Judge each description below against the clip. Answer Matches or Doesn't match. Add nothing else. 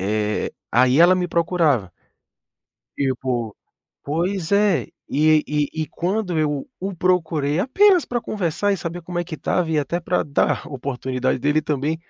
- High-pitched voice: Doesn't match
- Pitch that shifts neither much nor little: Matches